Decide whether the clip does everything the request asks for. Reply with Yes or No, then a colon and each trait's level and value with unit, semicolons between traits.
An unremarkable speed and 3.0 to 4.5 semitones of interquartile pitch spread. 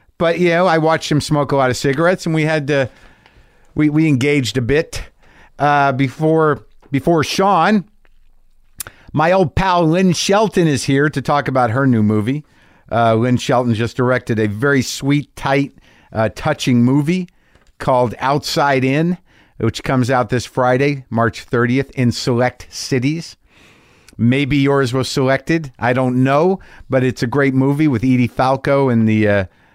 Yes: average, 160 wpm; average, 3.4 semitones